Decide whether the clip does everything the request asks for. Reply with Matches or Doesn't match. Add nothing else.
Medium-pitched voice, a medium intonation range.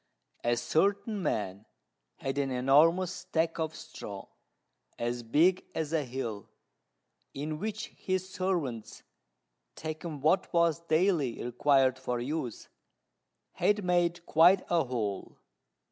Doesn't match